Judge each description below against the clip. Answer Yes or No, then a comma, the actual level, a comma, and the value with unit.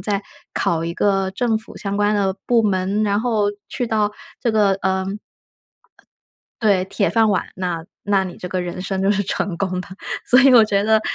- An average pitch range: No, narrow, 2.3 semitones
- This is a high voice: Yes, high, 200 Hz